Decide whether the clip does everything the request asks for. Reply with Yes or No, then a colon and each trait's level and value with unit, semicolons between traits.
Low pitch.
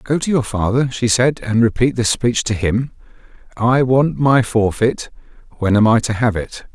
Yes: low, 120 Hz